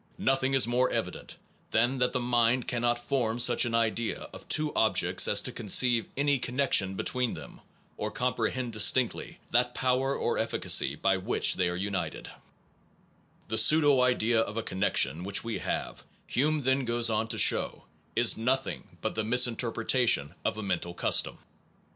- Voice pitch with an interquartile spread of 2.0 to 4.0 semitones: Yes, narrow, 2.6 semitones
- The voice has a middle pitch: No, low, 120 Hz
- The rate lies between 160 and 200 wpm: Yes, average, 165 wpm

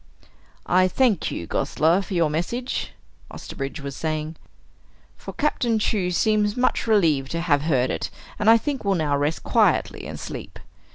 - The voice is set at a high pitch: No, medium, 175 Hz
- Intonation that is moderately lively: No, wide, 5.9 semitones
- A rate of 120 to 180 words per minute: Yes, average, 160 wpm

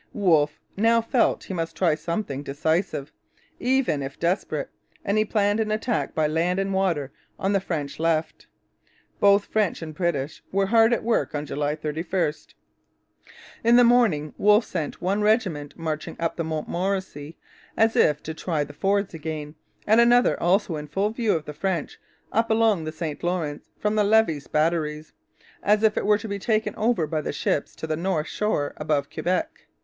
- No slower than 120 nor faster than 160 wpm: No, average, 175 wpm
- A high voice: No, medium, 175 Hz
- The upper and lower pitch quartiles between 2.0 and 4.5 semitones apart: No, wide, 5.4 semitones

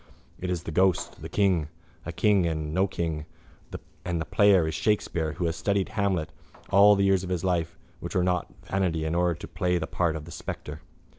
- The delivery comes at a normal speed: No, fast, 210 wpm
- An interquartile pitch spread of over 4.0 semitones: No, average, 3.0 semitones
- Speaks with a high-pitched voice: No, very low, 90 Hz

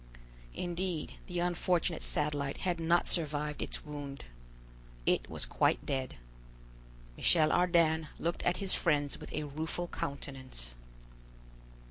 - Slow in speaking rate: Yes, slow, 115 wpm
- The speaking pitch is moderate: Yes, medium, 160 Hz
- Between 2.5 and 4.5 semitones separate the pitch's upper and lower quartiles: Yes, average, 3.3 semitones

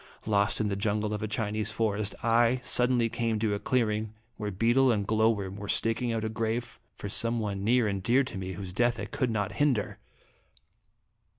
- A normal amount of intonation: No, narrow, 2.3 semitones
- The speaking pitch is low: Yes, low, 110 Hz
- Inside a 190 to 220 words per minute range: Yes, average, 200 wpm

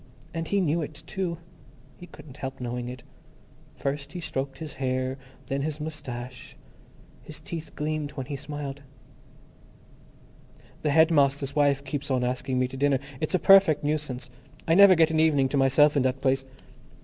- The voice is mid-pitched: Yes, medium, 145 Hz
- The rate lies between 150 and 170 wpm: Yes, average, 165 wpm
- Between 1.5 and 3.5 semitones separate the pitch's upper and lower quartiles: Yes, average, 2.9 semitones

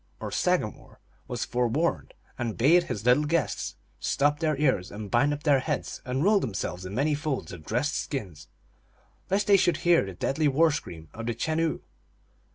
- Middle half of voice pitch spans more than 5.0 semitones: Yes, wide, 5.5 semitones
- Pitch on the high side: No, medium, 140 Hz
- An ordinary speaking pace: Yes, average, 175 wpm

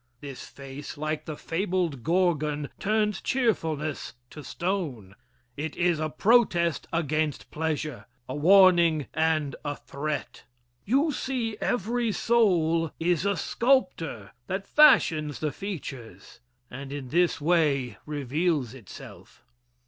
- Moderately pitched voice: Yes, medium, 160 Hz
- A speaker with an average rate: No, slow, 115 wpm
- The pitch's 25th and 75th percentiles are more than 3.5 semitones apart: Yes, average, 4.5 semitones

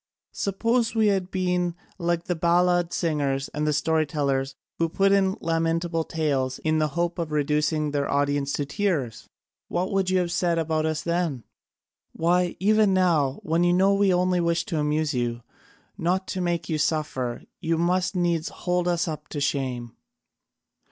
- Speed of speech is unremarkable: Yes, average, 165 wpm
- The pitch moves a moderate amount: Yes, average, 3.2 semitones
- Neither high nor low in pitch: Yes, medium, 165 Hz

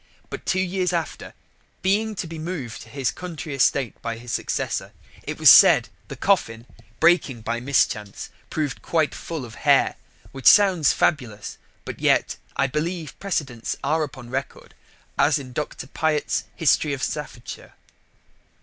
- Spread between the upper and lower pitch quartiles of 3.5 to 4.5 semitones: No, average, 4.9 semitones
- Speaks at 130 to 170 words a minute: Yes, average, 150 wpm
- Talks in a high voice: No, medium, 150 Hz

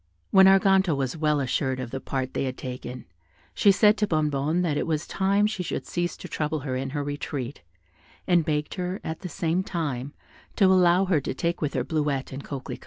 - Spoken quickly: Yes, fast, 210 wpm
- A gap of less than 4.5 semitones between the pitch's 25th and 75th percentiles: No, average, 4.9 semitones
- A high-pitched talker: No, medium, 155 Hz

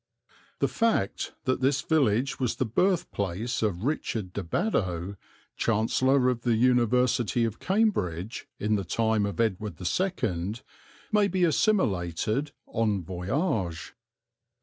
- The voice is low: Yes, low, 115 Hz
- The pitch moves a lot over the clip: Yes, wide, 5.7 semitones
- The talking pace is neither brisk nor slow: No, slow, 120 wpm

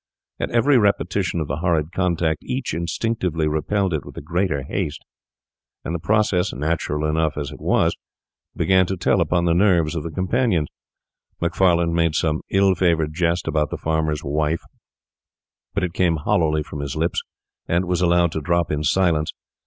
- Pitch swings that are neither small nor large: Yes, average, 3.0 semitones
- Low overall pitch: Yes, very low, 85 Hz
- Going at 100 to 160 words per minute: No, average, 170 wpm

